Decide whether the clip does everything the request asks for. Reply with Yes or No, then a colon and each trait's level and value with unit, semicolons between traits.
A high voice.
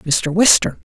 No: medium, 170 Hz